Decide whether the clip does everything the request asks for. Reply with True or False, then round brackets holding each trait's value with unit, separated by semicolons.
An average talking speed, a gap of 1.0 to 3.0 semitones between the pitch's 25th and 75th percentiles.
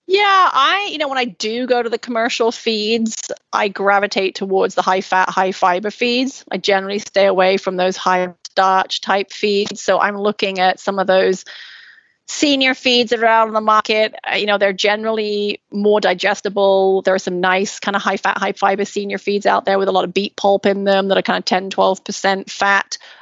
False (210 wpm; 2.4 semitones)